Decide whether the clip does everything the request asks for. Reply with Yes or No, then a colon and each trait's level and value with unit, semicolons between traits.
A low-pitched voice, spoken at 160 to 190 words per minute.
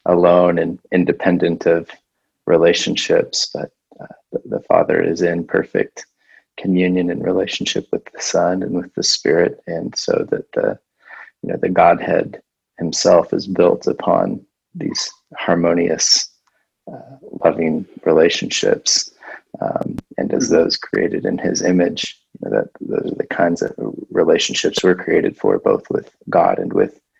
No: very low, 90 Hz; average, 145 wpm